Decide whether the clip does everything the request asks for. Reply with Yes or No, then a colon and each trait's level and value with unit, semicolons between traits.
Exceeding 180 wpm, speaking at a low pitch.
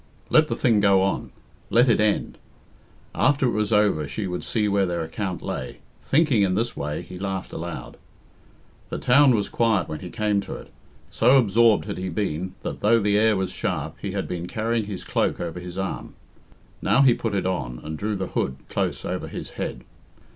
Yes: average, 200 wpm; low, 100 Hz